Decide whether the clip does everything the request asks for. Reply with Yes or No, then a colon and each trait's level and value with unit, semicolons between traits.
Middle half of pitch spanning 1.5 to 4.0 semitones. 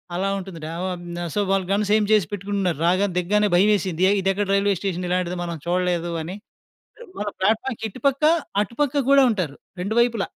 Yes: average, 2.7 semitones